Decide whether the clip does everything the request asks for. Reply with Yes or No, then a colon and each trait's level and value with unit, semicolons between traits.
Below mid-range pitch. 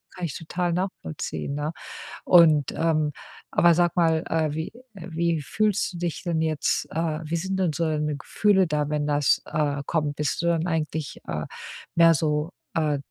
No: medium, 160 Hz